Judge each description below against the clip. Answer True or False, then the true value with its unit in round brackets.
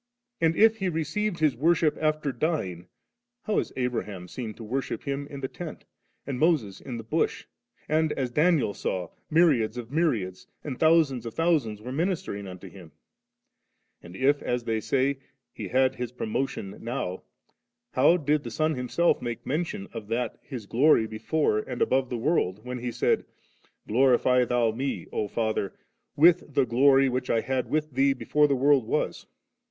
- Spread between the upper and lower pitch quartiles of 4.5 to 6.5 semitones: True (5.1 semitones)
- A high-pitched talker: False (130 Hz)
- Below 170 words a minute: False (175 wpm)